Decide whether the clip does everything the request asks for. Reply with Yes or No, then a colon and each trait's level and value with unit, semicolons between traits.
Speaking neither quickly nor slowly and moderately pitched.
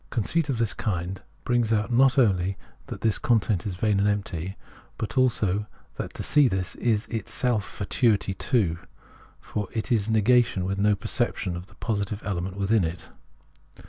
No: average, 170 wpm; low, 105 Hz